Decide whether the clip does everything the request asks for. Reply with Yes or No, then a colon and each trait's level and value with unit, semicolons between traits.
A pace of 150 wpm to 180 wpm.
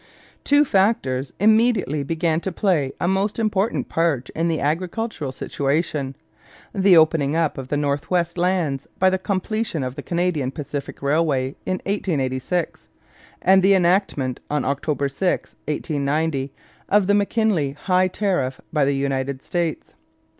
No: average, 140 wpm